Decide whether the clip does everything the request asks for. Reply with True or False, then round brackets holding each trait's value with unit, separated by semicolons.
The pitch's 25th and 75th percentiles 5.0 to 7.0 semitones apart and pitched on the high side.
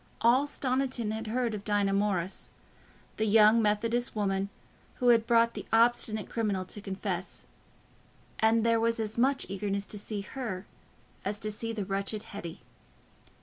False (2.4 semitones; 215 Hz)